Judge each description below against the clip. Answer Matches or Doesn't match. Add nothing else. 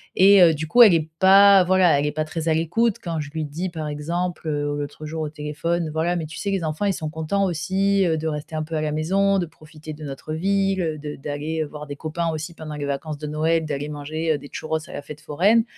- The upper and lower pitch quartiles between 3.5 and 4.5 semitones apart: Doesn't match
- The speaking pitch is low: Doesn't match